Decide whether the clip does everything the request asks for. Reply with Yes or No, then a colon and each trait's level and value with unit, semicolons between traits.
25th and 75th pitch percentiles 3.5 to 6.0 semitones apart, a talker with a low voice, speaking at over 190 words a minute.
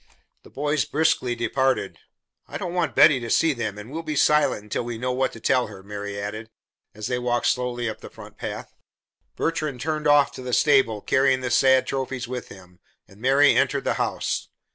Yes: average, 3.9 semitones; low, 125 Hz; average, 200 wpm